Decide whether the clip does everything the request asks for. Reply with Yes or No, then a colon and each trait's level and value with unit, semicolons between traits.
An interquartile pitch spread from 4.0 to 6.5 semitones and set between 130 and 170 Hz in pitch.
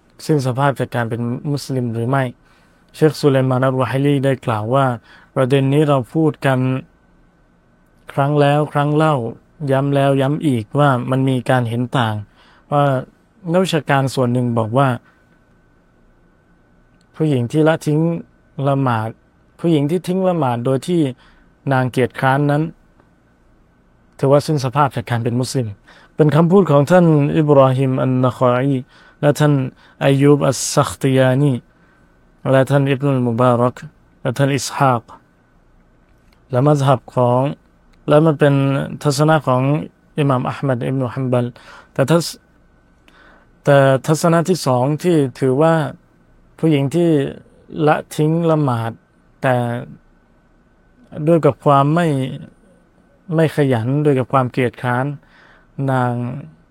No: average, 3.0 semitones; low, 135 Hz